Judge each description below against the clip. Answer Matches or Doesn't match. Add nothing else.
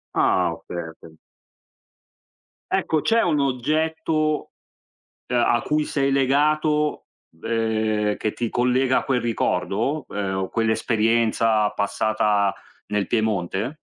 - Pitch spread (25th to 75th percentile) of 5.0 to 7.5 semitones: Matches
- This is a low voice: Matches